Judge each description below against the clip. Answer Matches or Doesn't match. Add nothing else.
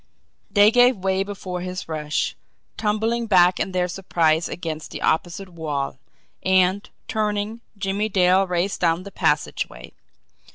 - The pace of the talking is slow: Matches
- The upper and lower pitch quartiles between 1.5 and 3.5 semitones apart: Matches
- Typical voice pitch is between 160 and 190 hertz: Matches